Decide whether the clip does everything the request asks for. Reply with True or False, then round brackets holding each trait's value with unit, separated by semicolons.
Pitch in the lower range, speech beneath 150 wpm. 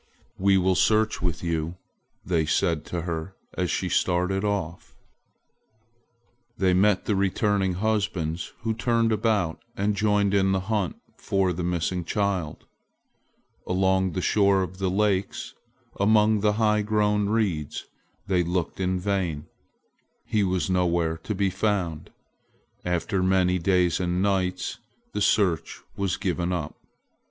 True (95 Hz; 135 wpm)